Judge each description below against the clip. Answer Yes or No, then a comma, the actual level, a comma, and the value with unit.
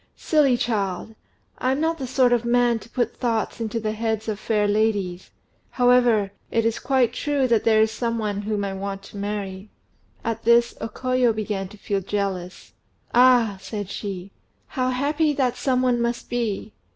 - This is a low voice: No, high, 225 Hz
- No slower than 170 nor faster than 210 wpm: Yes, average, 175 wpm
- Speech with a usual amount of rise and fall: Yes, average, 3.3 semitones